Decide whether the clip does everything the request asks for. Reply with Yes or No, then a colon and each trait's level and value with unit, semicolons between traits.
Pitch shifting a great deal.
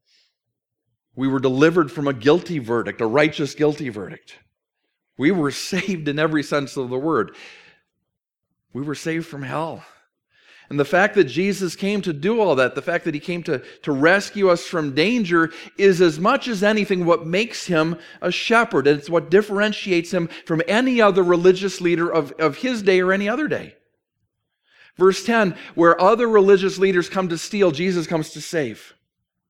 No: average, 4.3 semitones